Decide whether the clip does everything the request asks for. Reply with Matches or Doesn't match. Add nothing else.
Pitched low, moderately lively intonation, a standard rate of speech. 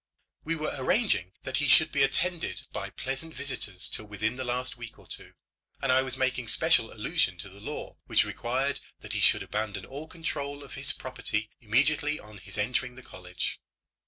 Matches